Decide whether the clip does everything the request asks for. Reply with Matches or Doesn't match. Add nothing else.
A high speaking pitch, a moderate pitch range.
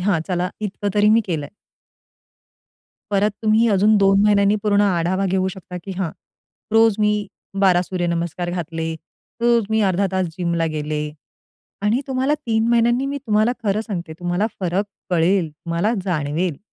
Matches